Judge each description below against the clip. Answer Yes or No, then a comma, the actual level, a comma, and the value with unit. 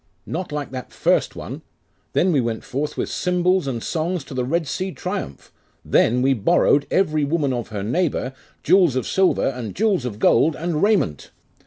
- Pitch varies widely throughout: Yes, wide, 6.2 semitones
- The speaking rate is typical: Yes, average, 180 wpm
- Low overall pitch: No, medium, 150 Hz